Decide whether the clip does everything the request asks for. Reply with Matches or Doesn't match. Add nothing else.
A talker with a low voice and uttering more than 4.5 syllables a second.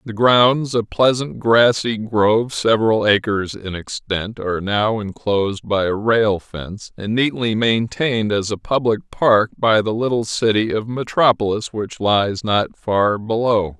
Doesn't match